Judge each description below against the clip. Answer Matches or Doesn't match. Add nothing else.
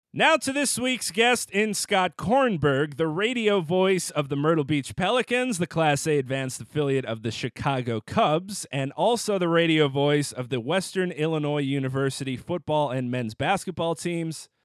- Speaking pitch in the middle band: Matches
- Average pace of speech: Matches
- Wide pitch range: Matches